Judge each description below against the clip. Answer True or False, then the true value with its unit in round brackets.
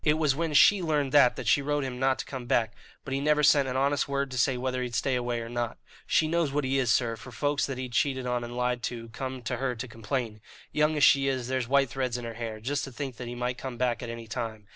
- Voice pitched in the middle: False (130 Hz)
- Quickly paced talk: True (285 wpm)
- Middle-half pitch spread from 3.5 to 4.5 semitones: False (2.6 semitones)